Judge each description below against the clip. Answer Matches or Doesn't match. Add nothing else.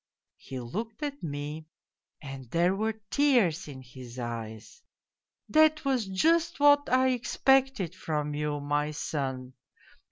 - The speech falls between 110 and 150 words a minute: Matches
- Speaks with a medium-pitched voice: Matches